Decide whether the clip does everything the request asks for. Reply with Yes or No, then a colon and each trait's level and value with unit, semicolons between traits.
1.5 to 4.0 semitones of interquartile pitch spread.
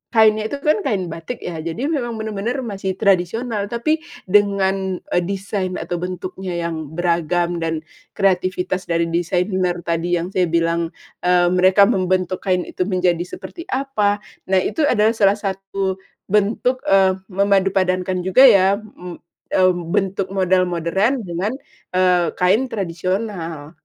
Yes: average, 2.7 semitones